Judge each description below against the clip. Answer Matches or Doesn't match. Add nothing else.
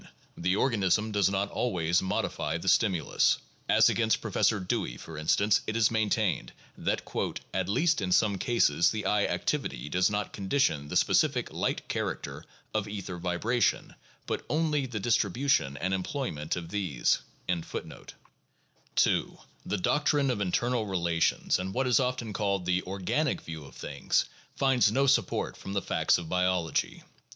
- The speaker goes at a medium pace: Matches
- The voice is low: Matches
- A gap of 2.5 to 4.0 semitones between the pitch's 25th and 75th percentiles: Doesn't match